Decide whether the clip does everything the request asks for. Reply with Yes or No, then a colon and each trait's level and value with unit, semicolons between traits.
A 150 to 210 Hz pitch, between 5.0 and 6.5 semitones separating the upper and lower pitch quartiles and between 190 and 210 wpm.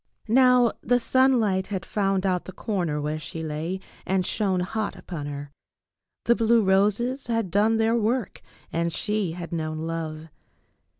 No: high, 190 Hz; average, 5.3 semitones; average, 155 wpm